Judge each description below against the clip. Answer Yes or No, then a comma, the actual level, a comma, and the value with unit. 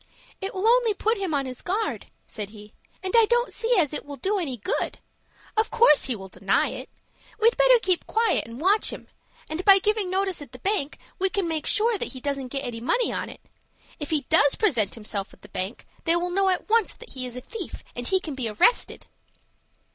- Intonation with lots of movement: Yes, wide, 8.7 semitones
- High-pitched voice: Yes, very high, 355 Hz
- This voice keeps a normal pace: No, fast, 225 wpm